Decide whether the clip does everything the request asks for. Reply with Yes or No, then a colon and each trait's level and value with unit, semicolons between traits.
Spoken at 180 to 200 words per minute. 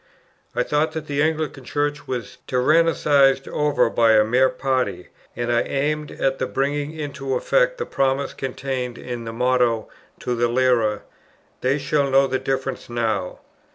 No: average, 155 wpm